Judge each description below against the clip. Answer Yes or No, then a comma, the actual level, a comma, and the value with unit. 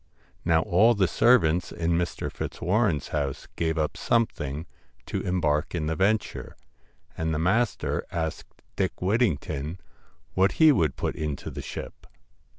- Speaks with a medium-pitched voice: No, very low, 85 Hz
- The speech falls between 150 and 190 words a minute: No, average, 140 wpm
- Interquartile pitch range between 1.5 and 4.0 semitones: No, average, 4.6 semitones